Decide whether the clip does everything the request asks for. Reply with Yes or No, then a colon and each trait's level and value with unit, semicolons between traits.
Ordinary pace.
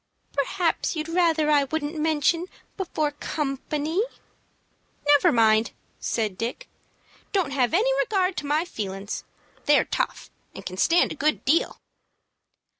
No: slow, 125 wpm